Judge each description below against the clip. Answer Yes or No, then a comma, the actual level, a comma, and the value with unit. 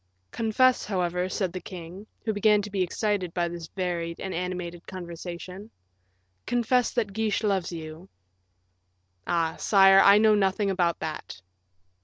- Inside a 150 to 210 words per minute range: No, average, 140 wpm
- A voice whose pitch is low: No, medium, 185 Hz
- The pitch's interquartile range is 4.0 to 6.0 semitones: No, average, 3.2 semitones